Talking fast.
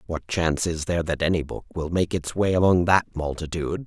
Yes: fast, 215 wpm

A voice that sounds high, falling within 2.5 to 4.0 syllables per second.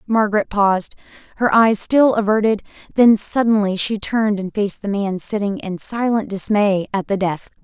No: high, 205 Hz; 5.0 syllables/s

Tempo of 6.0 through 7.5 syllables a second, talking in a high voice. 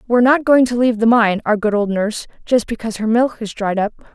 Yes: 6.5 syllables/s; high, 225 Hz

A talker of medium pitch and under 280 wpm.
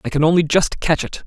No: medium, 165 Hz; fast, 285 wpm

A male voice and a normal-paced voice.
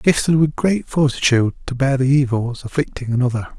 Yes: male; average, 170 wpm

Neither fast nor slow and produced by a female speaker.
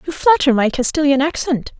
Yes: average, 165 wpm; female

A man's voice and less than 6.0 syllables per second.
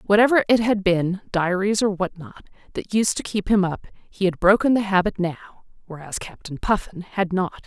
No: female; 4.8 syllables/s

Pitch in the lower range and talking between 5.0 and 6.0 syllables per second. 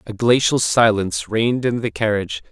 Yes: low, 115 Hz; 5.6 syllables/s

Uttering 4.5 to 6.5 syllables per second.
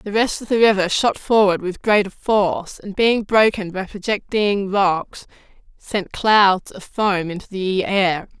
No: 4.1 syllables/s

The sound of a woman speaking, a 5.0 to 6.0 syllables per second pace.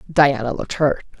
Yes: female; 5.6 syllables/s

